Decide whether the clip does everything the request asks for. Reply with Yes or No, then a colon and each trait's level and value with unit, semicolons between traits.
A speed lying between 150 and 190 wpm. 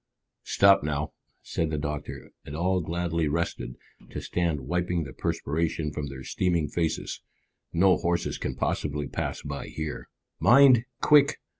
No: average, 140 wpm